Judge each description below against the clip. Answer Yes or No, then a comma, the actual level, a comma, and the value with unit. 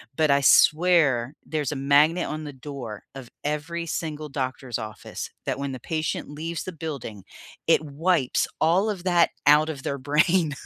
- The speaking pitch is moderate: Yes, medium, 150 Hz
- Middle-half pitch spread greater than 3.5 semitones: No, average, 3.2 semitones